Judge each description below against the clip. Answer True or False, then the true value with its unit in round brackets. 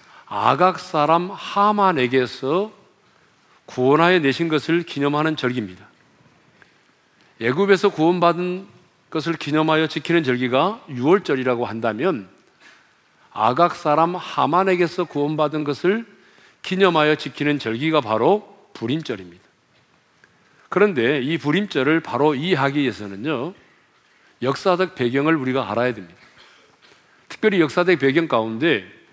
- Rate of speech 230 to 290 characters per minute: True (275 characters per minute)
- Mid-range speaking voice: True (160 Hz)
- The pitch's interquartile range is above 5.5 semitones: False (5.1 semitones)